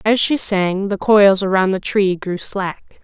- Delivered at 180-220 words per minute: Yes, average, 200 wpm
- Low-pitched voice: No, high, 195 Hz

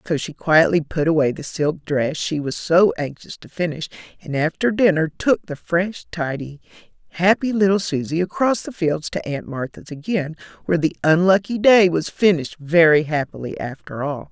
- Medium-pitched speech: Yes, medium, 165 Hz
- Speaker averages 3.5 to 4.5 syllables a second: No, 5.0 syllables/s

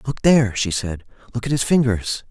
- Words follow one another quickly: Yes, fast, 210 wpm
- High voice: No, low, 115 Hz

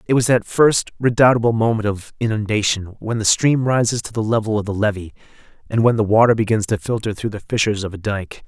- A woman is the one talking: No, male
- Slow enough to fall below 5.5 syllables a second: No, 5.9 syllables/s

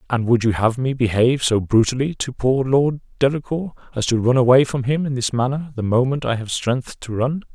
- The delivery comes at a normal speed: No, fast, 225 wpm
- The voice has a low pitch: Yes, low, 125 Hz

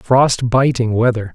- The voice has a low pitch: Yes, low, 120 Hz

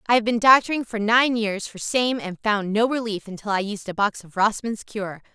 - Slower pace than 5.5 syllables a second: Yes, 5.2 syllables/s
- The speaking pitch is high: Yes, high, 215 Hz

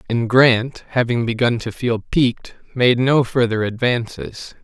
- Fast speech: No, average, 140 wpm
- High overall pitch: No, low, 120 Hz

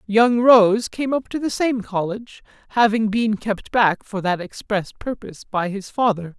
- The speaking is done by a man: Yes, male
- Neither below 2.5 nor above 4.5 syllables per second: Yes, 4.4 syllables/s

